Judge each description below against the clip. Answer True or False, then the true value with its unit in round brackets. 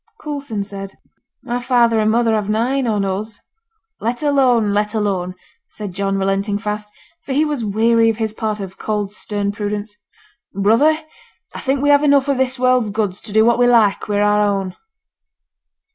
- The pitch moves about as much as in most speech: True (3.2 semitones)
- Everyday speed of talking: True (175 wpm)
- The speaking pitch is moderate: False (215 Hz)